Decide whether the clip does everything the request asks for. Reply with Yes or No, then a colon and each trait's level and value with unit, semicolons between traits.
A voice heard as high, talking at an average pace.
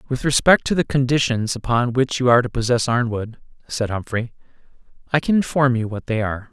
No: low, 125 Hz; average, 195 wpm